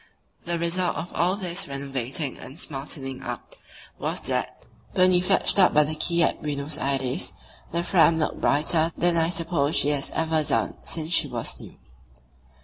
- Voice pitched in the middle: Yes, medium, 160 Hz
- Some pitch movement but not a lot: Yes, average, 3.4 semitones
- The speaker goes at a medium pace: Yes, average, 170 wpm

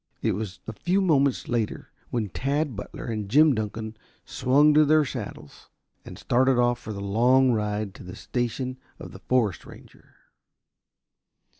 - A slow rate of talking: No, average, 155 wpm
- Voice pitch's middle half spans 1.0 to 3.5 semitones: No, average, 4.1 semitones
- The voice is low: Yes, low, 120 Hz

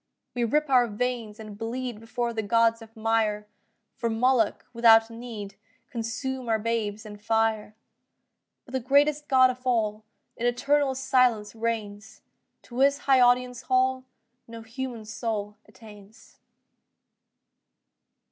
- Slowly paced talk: Yes, slow, 130 wpm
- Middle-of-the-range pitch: No, high, 230 Hz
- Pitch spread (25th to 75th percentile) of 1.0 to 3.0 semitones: Yes, narrow, 2.6 semitones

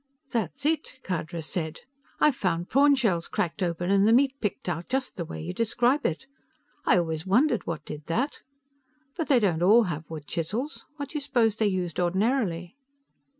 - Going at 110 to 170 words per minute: No, average, 185 wpm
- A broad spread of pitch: Yes, wide, 7.1 semitones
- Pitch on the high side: Yes, high, 195 Hz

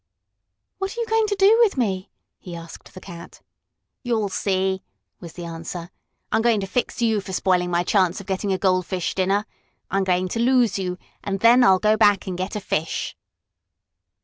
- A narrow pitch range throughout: No, average, 3.8 semitones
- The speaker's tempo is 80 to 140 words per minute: No, average, 190 wpm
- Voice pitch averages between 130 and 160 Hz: No, high, 195 Hz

